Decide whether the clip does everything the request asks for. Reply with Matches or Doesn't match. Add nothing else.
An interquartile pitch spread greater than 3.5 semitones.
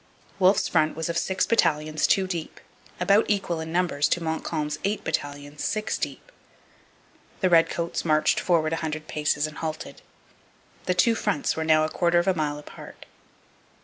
Doesn't match